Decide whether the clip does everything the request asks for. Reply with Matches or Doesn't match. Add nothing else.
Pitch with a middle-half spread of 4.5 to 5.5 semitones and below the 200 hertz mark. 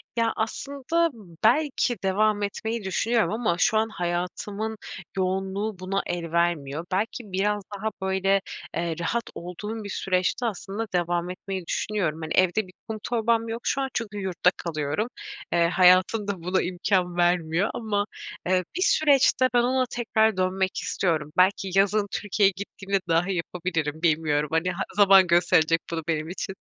Doesn't match